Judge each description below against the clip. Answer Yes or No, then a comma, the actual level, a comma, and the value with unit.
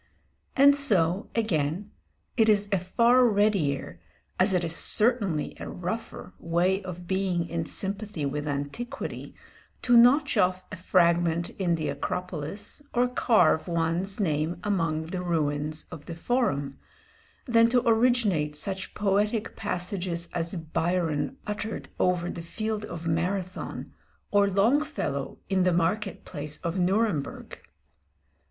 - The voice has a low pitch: No, medium, 185 Hz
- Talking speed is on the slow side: Yes, slow, 130 wpm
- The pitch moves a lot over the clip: No, average, 4.3 semitones